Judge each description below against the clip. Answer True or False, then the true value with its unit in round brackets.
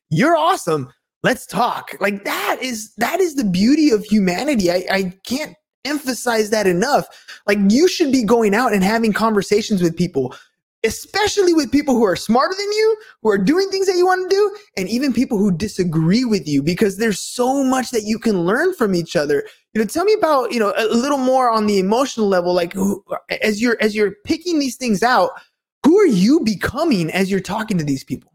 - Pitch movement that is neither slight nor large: False (6.9 semitones)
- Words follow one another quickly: True (210 wpm)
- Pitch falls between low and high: False (225 Hz)